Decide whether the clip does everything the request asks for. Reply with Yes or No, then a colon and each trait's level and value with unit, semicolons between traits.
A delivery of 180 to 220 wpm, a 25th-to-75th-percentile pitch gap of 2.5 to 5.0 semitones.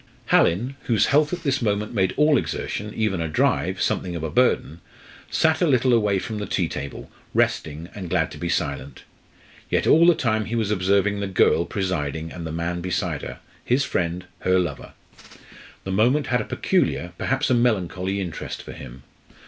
No: average, 185 wpm; wide, 5.6 semitones